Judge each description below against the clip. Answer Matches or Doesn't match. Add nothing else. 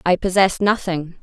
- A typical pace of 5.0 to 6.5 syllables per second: Doesn't match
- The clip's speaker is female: Matches